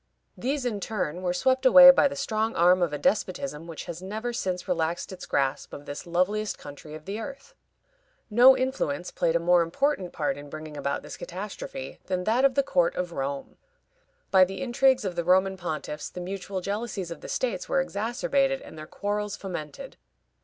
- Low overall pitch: No, medium, 185 Hz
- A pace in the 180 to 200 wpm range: Yes, average, 190 wpm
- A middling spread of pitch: No, wide, 6.1 semitones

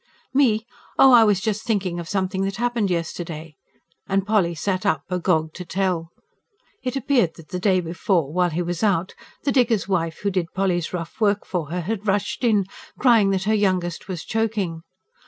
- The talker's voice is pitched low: No, high, 190 Hz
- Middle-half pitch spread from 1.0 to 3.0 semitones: No, average, 3.7 semitones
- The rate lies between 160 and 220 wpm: Yes, average, 185 wpm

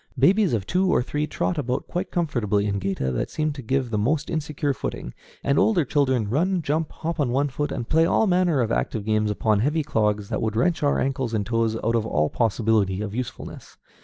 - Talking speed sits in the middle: No, fast, 215 wpm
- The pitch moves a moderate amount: No, wide, 6.0 semitones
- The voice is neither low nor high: No, low, 125 Hz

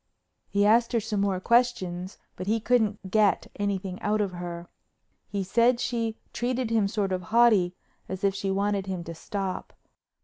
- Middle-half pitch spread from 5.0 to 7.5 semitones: No, average, 3.2 semitones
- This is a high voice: Yes, high, 200 Hz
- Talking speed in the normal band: Yes, average, 170 wpm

